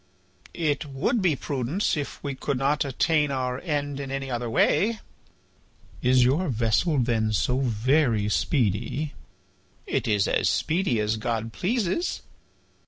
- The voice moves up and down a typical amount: Yes, average, 4.3 semitones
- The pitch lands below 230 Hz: Yes, low, 135 Hz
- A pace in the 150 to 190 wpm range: No, slow, 135 wpm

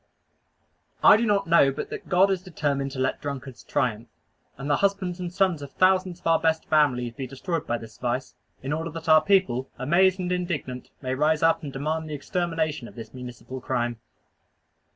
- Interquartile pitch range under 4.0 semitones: No, average, 5.2 semitones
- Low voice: No, medium, 155 Hz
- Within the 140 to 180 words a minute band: No, average, 195 wpm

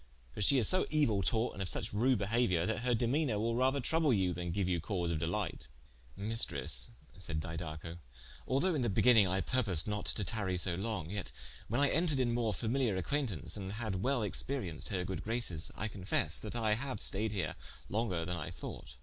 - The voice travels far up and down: No, average, 5.0 semitones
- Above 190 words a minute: Yes, average, 200 wpm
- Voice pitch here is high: No, low, 105 Hz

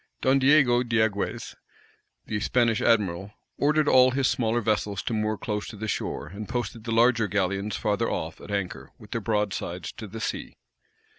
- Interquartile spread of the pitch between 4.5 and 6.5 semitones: No, average, 2.9 semitones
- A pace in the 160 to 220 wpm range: Yes, average, 170 wpm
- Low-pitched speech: Yes, low, 110 Hz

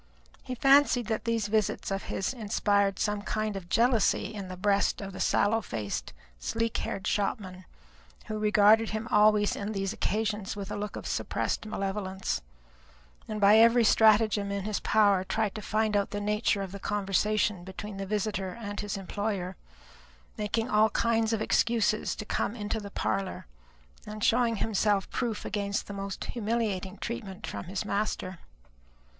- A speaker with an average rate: Yes, average, 160 wpm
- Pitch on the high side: Yes, high, 210 Hz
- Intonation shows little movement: Yes, narrow, 1.8 semitones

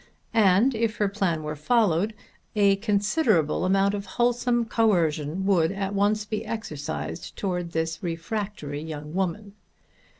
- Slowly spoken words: Yes, slow, 130 wpm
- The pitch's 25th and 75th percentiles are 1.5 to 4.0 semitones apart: No, average, 4.5 semitones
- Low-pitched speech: No, high, 195 Hz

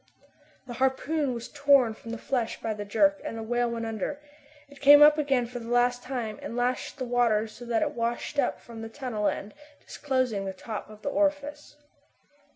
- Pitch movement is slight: No, average, 3.5 semitones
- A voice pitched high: Yes, high, 245 Hz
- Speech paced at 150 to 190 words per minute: No, average, 200 wpm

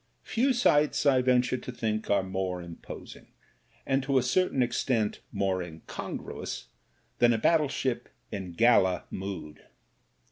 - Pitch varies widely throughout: Yes, wide, 5.9 semitones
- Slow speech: Yes, slow, 130 wpm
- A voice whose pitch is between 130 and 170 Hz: No, low, 115 Hz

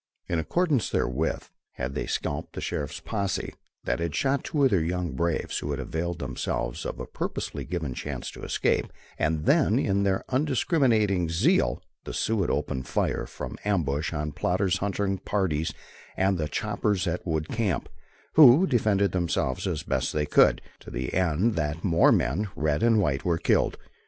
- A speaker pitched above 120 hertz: No, very low, 90 Hz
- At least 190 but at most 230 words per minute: No, average, 175 wpm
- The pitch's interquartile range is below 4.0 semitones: No, average, 5.2 semitones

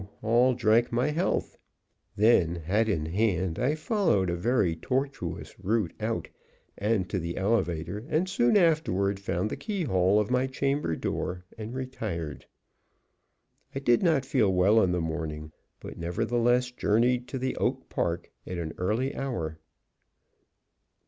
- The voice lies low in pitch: Yes, low, 110 Hz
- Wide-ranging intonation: Yes, wide, 6.3 semitones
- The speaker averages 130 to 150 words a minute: Yes, average, 140 wpm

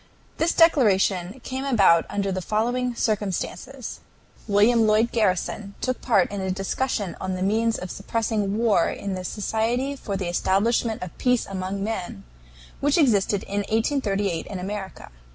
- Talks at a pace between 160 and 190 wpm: No, average, 150 wpm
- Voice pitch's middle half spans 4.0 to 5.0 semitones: No, average, 3.5 semitones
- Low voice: No, high, 210 Hz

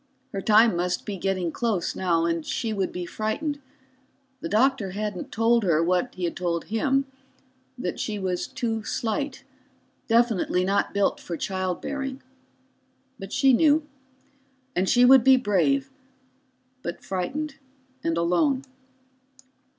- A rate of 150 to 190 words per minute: No, slow, 135 wpm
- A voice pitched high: Yes, high, 210 Hz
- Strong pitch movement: Yes, wide, 6.2 semitones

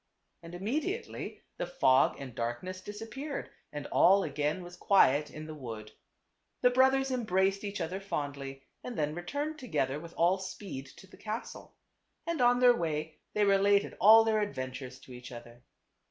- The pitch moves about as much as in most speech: No, wide, 7.7 semitones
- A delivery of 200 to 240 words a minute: No, average, 165 wpm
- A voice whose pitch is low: No, medium, 185 Hz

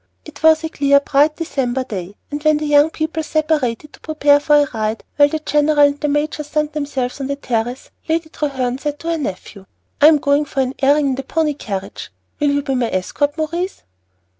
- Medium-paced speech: No, fast, 215 wpm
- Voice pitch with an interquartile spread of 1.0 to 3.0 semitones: Yes, narrow, 2.5 semitones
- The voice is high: Yes, very high, 290 Hz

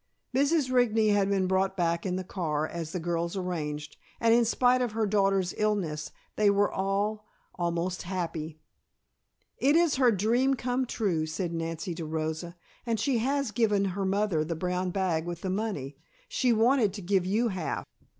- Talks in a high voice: Yes, high, 195 Hz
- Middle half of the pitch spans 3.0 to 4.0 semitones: No, average, 4.7 semitones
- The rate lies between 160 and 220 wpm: Yes, average, 180 wpm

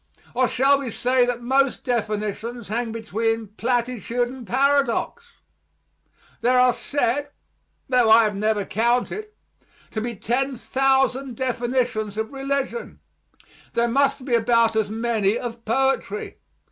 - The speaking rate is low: Yes, slow, 120 wpm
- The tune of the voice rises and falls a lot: No, average, 2.8 semitones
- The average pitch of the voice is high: Yes, high, 240 Hz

